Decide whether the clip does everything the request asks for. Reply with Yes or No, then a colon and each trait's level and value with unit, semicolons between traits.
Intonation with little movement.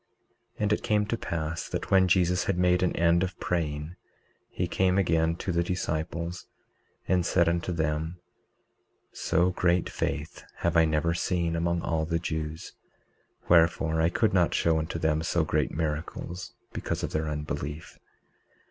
Yes: narrow, 2.0 semitones